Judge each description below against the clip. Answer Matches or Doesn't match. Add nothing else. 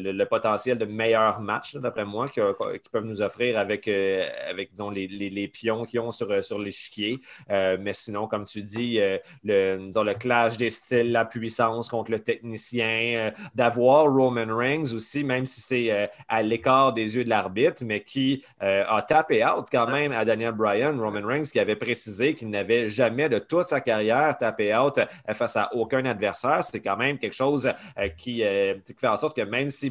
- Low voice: Matches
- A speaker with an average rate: Matches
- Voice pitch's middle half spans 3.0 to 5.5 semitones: Matches